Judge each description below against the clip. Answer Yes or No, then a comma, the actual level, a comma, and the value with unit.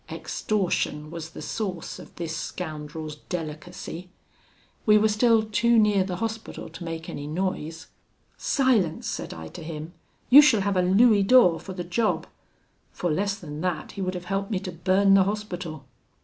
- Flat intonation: No, average, 4.3 semitones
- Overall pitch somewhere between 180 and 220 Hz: Yes, medium, 185 Hz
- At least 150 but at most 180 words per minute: Yes, average, 170 wpm